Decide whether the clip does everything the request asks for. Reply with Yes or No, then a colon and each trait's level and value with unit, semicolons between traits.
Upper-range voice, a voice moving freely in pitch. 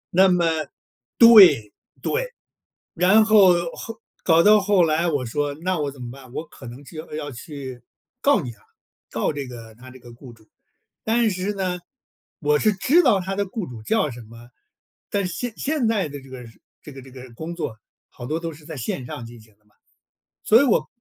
No: medium, 155 Hz; wide, 7.4 semitones